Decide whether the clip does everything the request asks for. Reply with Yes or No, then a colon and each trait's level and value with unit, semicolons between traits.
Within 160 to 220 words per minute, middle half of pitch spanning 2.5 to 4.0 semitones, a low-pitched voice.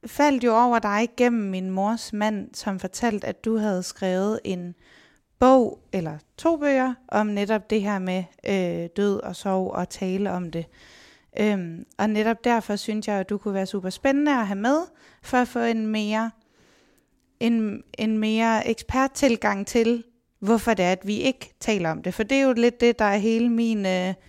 No: average, 190 wpm; average, 3.3 semitones; high, 215 Hz